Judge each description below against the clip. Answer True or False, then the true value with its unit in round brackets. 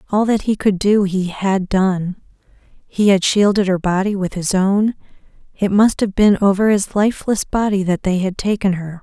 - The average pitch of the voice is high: True (195 Hz)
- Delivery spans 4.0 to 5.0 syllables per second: True (4.7 syllables/s)